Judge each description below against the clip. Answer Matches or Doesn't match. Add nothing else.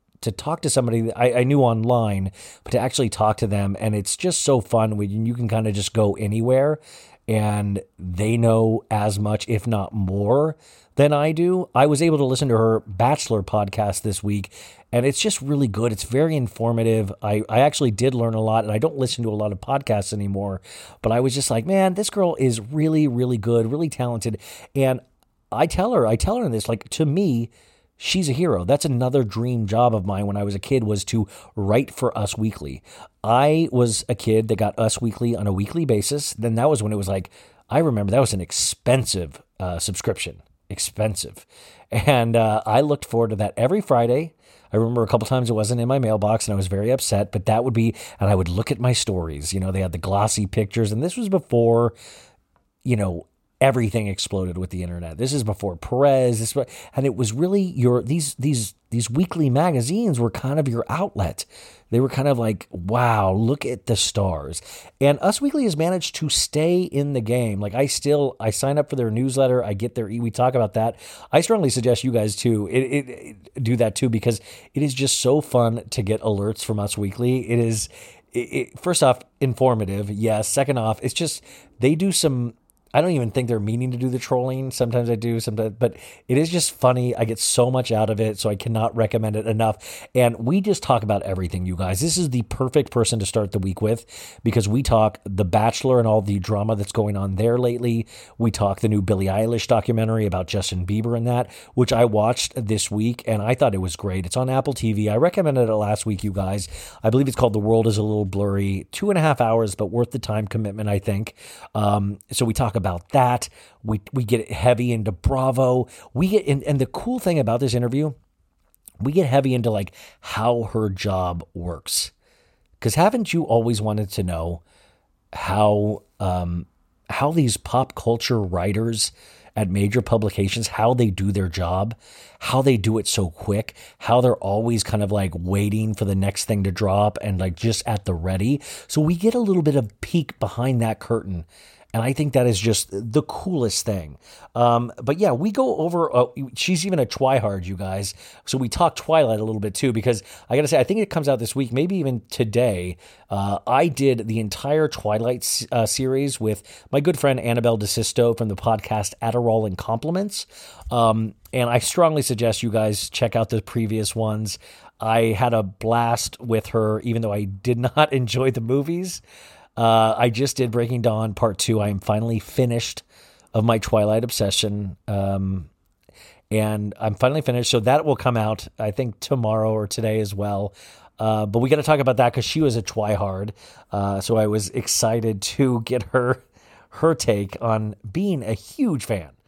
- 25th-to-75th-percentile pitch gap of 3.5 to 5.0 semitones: Matches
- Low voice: Matches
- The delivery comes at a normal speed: Doesn't match